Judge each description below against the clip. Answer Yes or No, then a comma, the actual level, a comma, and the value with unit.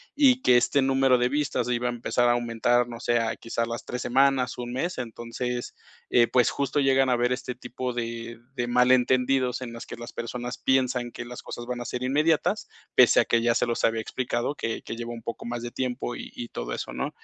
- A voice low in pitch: Yes, low, 125 Hz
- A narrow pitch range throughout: Yes, narrow, 1.5 semitones